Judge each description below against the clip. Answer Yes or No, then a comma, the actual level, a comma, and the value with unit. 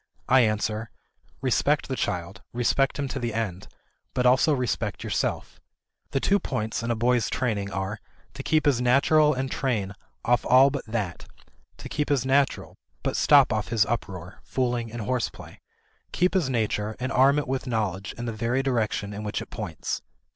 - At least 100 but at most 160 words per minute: No, average, 175 wpm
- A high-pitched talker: No, low, 120 Hz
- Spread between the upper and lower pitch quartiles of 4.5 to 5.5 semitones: No, average, 3.7 semitones